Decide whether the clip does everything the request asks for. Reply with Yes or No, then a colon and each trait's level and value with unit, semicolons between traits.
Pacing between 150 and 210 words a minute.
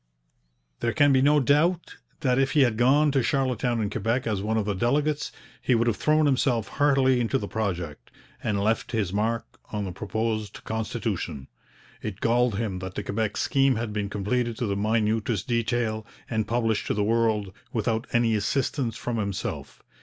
Yes: average, 180 wpm